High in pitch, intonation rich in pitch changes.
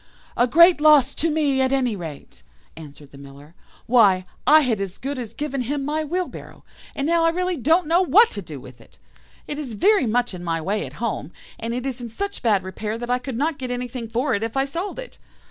Yes: very high, 250 Hz; wide, 6.3 semitones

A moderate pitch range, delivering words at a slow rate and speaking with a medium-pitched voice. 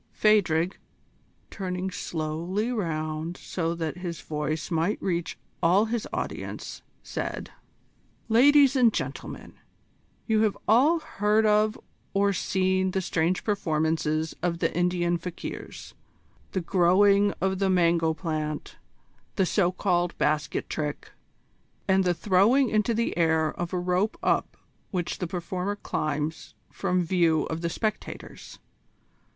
Yes: average, 3.7 semitones; slow, 125 wpm; medium, 180 Hz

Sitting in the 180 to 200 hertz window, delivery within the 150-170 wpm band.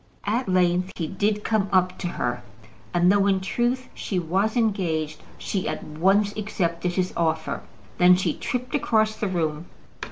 Yes: high, 190 Hz; average, 160 wpm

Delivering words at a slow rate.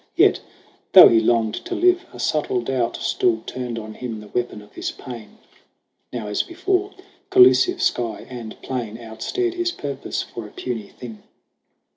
No: average, 160 wpm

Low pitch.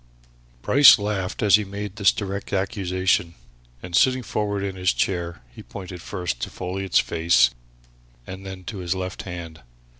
Yes: very low, 95 Hz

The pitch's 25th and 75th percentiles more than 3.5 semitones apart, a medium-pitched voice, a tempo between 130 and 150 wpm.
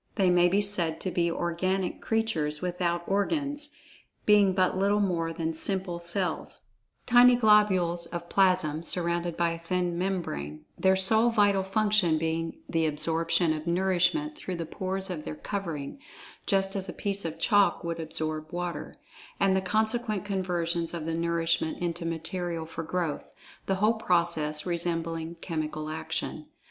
No: average, 2.9 semitones; medium, 175 Hz; average, 145 wpm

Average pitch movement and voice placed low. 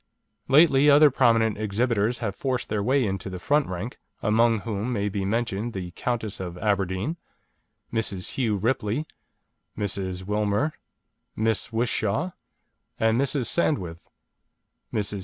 Yes: average, 3.8 semitones; low, 110 Hz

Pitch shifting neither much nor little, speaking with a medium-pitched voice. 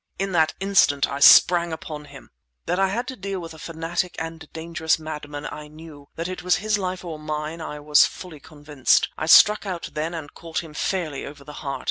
Yes: average, 3.1 semitones; medium, 160 Hz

